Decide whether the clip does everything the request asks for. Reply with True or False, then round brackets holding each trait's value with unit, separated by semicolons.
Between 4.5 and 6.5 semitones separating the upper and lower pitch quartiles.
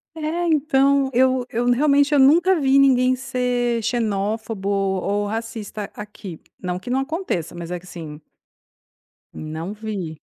True (5.5 semitones)